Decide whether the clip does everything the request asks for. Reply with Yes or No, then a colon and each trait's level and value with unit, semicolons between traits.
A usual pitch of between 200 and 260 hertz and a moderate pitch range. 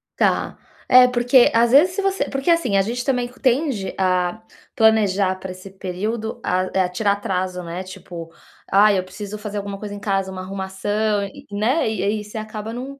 Yes: high, 205 Hz; average, 3.9 semitones